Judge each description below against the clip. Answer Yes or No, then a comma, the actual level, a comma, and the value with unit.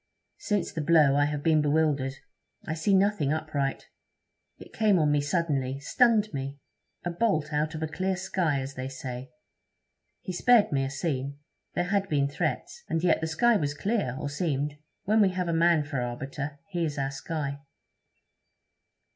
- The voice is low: No, medium, 155 Hz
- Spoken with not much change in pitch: No, average, 4.2 semitones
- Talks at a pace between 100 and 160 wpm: No, average, 175 wpm